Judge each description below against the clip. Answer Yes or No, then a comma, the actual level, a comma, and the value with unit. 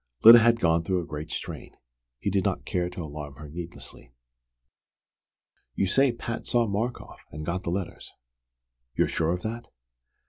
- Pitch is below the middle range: Yes, very low, 90 Hz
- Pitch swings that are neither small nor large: No, wide, 5.8 semitones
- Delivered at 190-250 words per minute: No, average, 165 wpm